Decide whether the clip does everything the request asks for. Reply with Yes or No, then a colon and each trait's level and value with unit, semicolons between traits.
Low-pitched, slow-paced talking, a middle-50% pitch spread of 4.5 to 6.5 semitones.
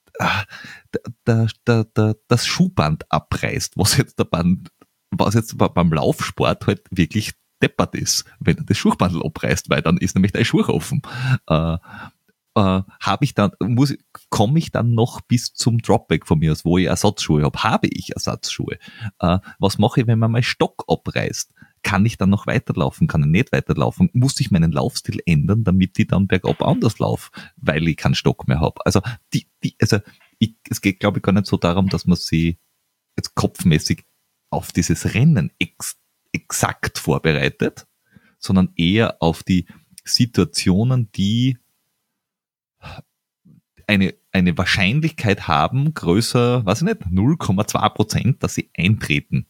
No: low, 100 Hz; average, 155 wpm; average, 4.8 semitones